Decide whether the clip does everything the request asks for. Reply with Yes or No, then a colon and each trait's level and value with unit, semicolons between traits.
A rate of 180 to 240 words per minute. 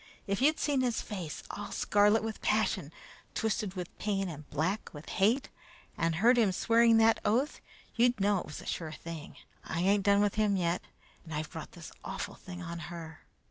Yes: average, 190 wpm